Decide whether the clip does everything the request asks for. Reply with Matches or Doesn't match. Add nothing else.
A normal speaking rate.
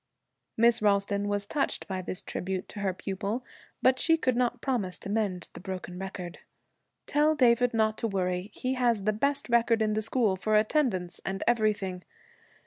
Matches